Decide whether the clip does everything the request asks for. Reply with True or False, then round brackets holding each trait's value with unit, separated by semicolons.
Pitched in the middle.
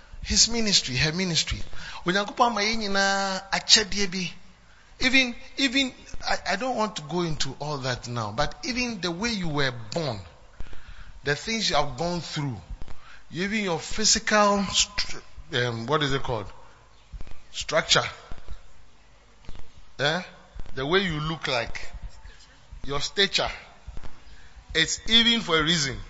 True (170 Hz)